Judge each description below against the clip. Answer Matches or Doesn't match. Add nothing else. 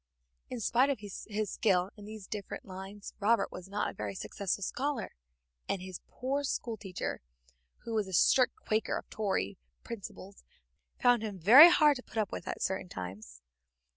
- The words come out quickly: Doesn't match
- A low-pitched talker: Doesn't match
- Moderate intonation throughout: Matches